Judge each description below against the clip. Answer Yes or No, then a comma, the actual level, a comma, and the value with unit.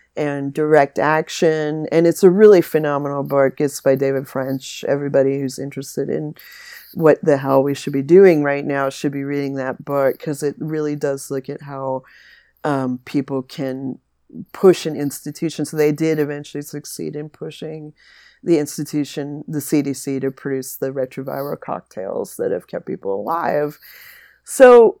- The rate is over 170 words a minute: No, average, 160 wpm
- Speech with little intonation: Yes, narrow, 2.2 semitones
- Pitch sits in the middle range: Yes, medium, 145 Hz